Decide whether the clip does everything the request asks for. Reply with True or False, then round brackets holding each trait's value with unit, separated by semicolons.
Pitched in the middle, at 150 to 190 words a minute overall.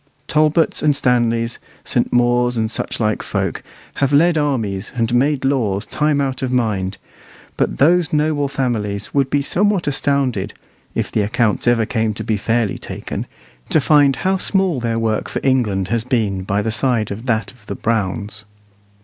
False (120 Hz; 170 wpm)